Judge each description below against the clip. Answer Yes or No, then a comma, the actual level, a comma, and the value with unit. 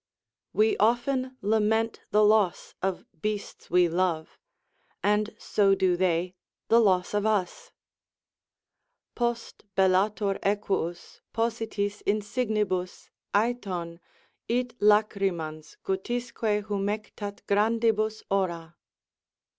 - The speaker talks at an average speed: No, slow, 90 wpm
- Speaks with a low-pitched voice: No, high, 205 Hz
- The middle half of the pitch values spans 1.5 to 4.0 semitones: Yes, average, 2.8 semitones